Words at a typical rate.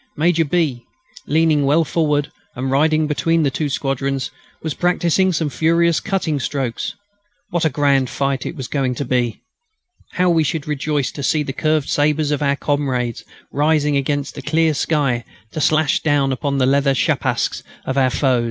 Yes: average, 170 wpm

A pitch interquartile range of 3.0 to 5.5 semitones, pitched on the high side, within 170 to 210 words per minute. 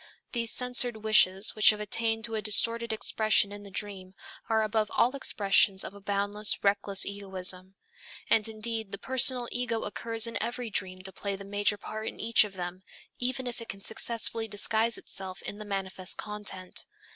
No: narrow, 2.5 semitones; high, 210 Hz; average, 180 wpm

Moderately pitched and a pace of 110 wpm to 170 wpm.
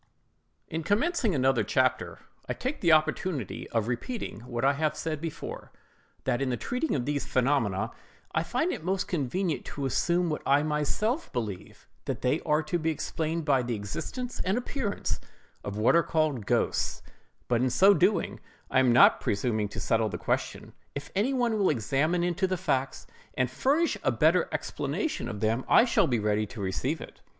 No: medium, 150 Hz; average, 180 wpm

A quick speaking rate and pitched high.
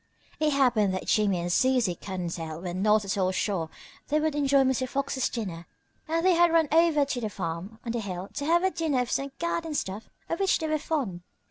Yes: fast, 220 wpm; high, 245 Hz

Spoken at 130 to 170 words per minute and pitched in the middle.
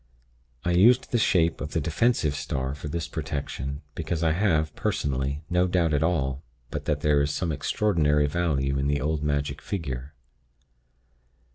No: average, 160 wpm; very low, 75 Hz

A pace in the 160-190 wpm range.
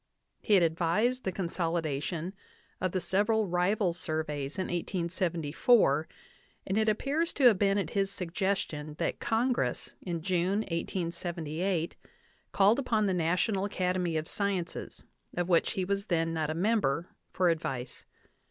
No: average, 140 wpm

